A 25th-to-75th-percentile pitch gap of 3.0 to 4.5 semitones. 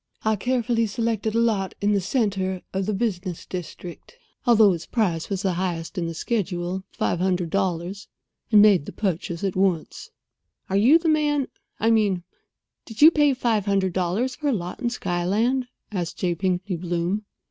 Yes: average, 4.2 semitones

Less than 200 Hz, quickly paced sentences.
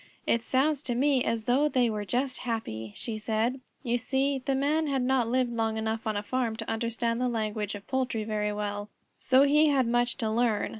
No: high, 235 Hz; fast, 210 wpm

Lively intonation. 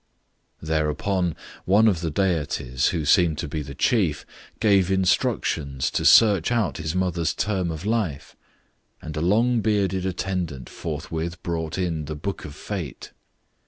No: average, 3.8 semitones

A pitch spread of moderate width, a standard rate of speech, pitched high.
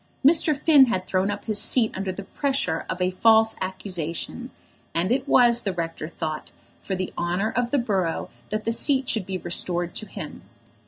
Yes: average, 4.8 semitones; average, 190 wpm; high, 200 Hz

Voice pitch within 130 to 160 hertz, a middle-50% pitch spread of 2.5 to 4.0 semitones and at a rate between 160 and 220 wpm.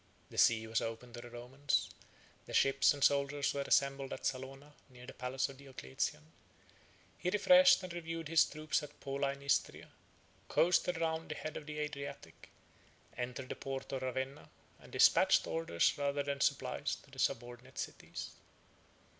Yes: medium, 140 Hz; average, 2.8 semitones; average, 165 wpm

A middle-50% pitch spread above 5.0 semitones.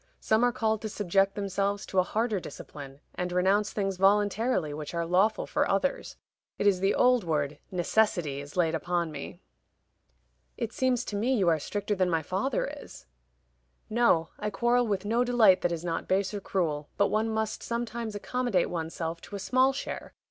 No: average, 4.2 semitones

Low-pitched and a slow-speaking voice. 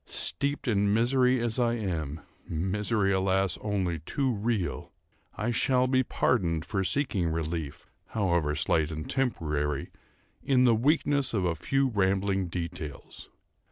Yes: low, 100 Hz; slow, 125 wpm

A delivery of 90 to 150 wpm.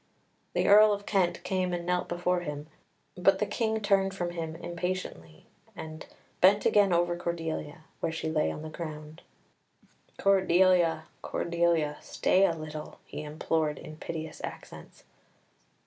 Yes: average, 140 wpm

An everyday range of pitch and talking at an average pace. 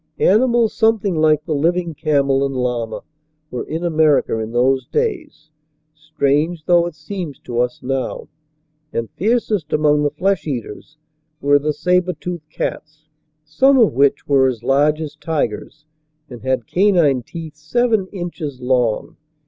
Yes: average, 4.6 semitones; average, 145 wpm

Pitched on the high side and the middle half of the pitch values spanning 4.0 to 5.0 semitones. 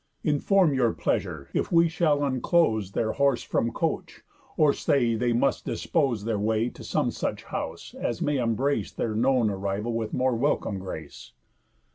No: low, 120 Hz; average, 4.5 semitones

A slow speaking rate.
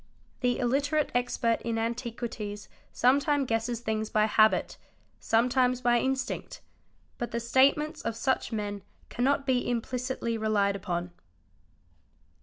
Yes: slow, 120 wpm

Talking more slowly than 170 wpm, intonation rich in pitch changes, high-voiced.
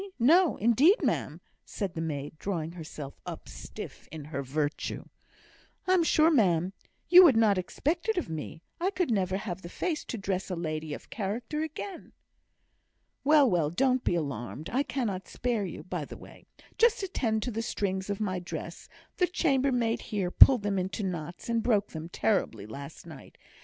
No: average, 175 wpm; wide, 7.9 semitones; high, 200 Hz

